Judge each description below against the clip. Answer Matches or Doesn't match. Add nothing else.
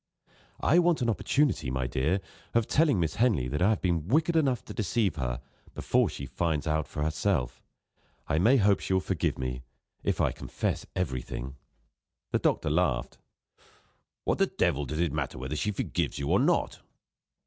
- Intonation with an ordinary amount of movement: Doesn't match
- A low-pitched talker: Matches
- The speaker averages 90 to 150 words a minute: Doesn't match